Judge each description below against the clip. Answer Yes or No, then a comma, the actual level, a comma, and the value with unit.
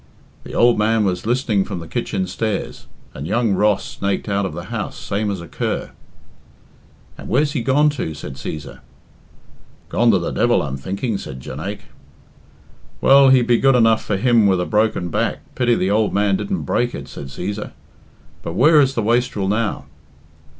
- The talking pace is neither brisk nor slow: Yes, average, 180 wpm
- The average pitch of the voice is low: Yes, low, 105 Hz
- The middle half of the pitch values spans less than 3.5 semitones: No, average, 4.2 semitones